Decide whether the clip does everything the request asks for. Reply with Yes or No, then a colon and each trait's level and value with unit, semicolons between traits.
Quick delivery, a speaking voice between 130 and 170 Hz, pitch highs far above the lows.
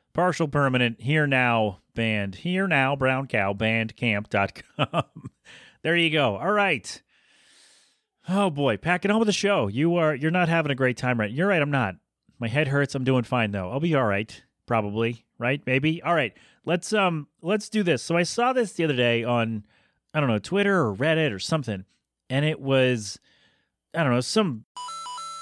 No: average, 185 wpm; medium, 140 Hz; wide, 6.5 semitones